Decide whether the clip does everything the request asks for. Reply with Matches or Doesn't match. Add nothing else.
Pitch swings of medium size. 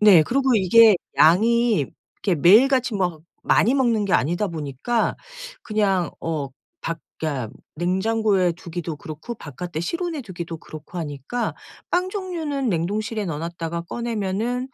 Doesn't match